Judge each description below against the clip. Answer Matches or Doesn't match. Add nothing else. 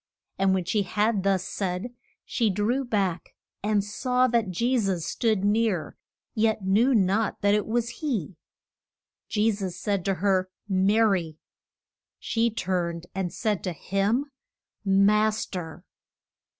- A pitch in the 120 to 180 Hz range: Doesn't match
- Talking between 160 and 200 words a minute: Doesn't match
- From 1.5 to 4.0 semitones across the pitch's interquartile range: Matches